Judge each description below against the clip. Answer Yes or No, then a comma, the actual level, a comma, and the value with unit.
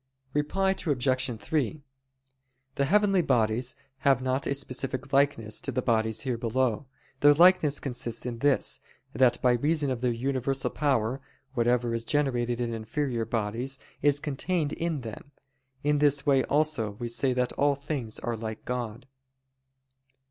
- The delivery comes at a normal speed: Yes, average, 150 wpm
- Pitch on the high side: No, low, 130 Hz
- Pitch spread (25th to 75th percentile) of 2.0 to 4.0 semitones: Yes, average, 3.5 semitones